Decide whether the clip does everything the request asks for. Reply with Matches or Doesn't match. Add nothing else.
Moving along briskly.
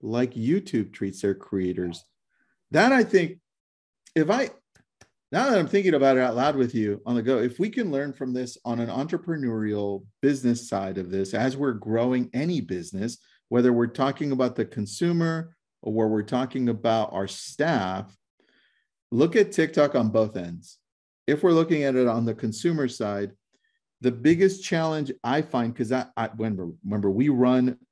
Doesn't match